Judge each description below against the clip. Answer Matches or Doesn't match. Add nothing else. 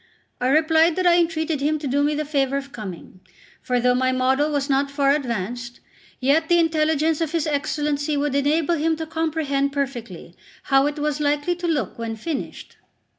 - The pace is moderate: Matches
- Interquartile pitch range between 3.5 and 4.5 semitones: Doesn't match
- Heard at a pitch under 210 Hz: Doesn't match